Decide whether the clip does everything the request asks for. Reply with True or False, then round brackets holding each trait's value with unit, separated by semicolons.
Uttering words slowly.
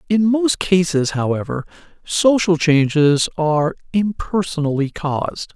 True (95 wpm)